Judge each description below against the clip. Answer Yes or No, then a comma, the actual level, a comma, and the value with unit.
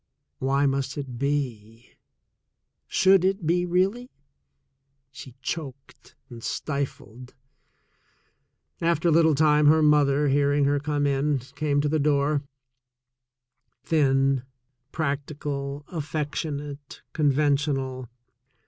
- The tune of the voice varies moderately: No, narrow, 2.1 semitones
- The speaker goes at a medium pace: No, slow, 100 wpm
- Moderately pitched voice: Yes, medium, 145 Hz